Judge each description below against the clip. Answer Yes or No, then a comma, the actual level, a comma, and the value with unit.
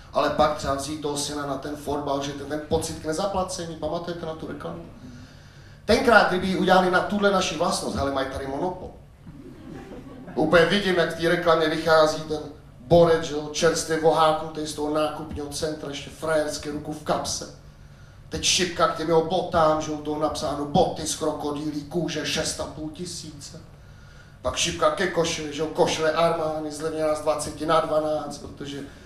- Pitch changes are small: Yes, narrow, 1.9 semitones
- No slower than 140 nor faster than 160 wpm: No, fast, 170 wpm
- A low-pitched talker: No, medium, 155 Hz